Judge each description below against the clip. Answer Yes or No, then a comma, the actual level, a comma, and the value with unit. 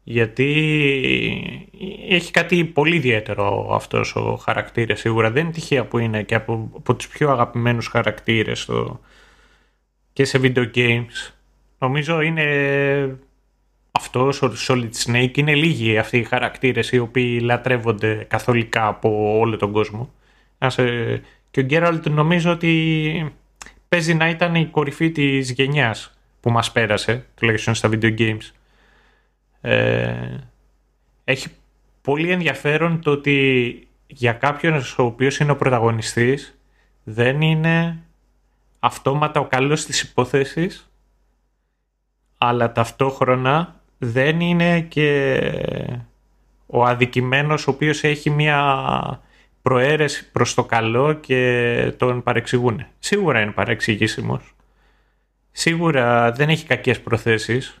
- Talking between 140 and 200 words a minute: No, slow, 115 wpm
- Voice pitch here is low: Yes, low, 130 Hz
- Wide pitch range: No, average, 4.3 semitones